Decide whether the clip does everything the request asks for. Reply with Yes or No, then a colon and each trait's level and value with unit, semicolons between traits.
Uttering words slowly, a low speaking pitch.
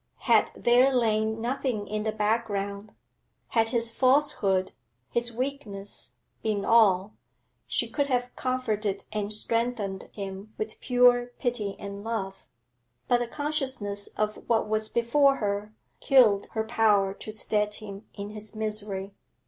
No: slow, 130 wpm; high, 215 Hz